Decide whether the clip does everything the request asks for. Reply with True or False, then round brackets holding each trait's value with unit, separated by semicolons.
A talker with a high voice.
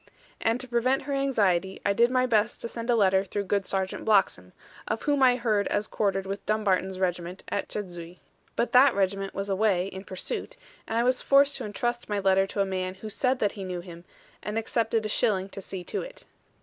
True (205 Hz)